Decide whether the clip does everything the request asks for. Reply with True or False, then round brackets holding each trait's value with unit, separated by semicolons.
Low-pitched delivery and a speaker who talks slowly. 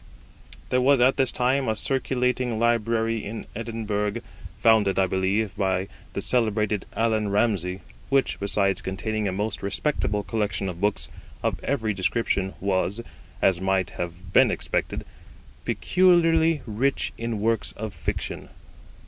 True (110 Hz; 130 wpm)